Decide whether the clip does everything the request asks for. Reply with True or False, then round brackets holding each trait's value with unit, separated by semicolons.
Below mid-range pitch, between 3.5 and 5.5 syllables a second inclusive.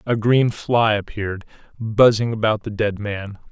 True (110 Hz; 4.4 syllables/s)